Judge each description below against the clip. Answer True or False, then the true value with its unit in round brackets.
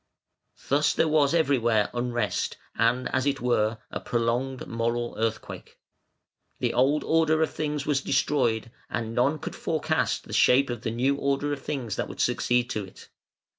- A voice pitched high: False (125 Hz)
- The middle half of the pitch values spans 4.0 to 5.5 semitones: False (3.4 semitones)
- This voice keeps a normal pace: True (165 wpm)